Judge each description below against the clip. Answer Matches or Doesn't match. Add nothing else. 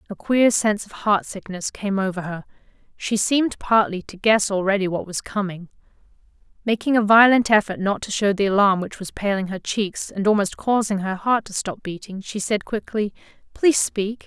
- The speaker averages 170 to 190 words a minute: Matches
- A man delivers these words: Doesn't match